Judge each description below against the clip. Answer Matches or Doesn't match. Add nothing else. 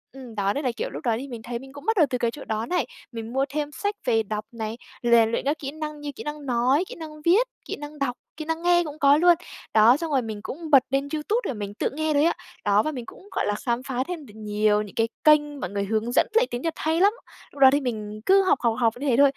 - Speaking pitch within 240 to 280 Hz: Matches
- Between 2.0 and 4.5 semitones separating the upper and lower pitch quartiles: Doesn't match